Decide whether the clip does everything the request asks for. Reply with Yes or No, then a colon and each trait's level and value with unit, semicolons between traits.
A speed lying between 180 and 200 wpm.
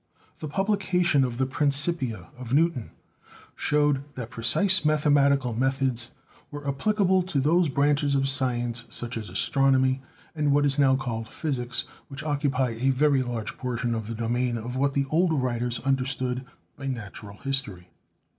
No: average, 155 wpm